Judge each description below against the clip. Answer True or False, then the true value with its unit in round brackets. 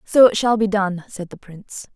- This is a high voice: True (200 Hz)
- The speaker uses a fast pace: True (245 wpm)